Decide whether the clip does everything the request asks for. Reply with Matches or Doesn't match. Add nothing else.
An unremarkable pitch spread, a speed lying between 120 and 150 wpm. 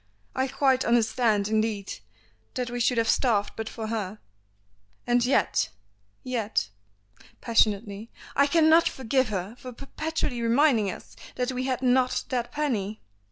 Matches